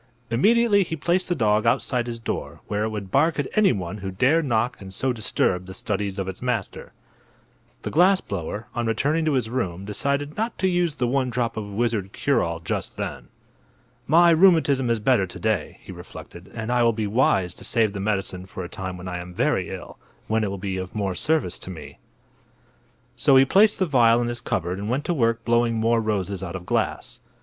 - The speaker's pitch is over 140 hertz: No, low, 115 Hz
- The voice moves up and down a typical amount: No, wide, 5.9 semitones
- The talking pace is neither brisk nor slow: No, fast, 215 wpm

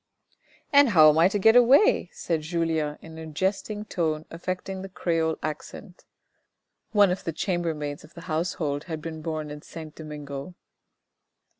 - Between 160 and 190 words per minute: Yes, average, 165 wpm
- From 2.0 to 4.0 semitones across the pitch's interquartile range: Yes, average, 3.2 semitones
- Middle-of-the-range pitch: Yes, medium, 165 Hz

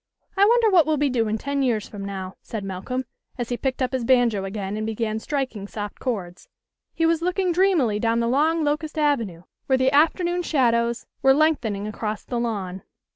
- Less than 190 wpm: No, average, 195 wpm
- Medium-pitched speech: No, high, 245 Hz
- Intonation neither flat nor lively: No, wide, 5.9 semitones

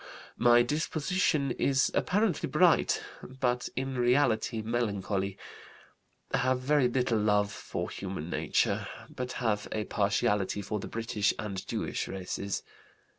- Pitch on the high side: No, low, 120 Hz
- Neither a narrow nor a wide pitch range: Yes, average, 4.1 semitones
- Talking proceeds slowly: Yes, slow, 120 wpm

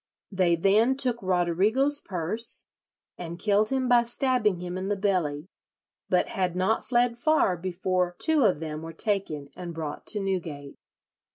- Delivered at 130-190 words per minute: Yes, average, 155 wpm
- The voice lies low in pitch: No, high, 190 Hz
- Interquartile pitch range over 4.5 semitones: Yes, average, 5.1 semitones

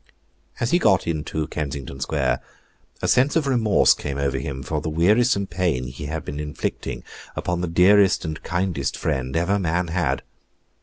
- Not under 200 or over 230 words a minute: No, average, 165 wpm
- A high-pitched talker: No, very low, 85 Hz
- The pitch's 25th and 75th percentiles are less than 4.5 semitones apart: No, average, 4.8 semitones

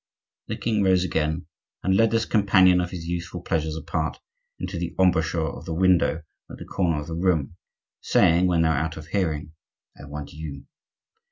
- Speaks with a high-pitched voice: No, very low, 85 Hz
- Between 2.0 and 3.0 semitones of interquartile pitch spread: Yes, narrow, 2.6 semitones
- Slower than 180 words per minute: No, average, 185 wpm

